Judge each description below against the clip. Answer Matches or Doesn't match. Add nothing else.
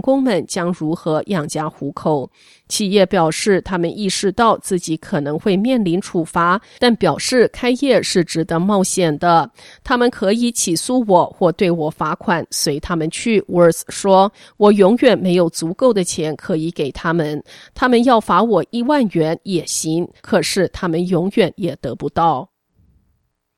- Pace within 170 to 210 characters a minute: Doesn't match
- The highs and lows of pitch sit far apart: Doesn't match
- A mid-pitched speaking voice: Matches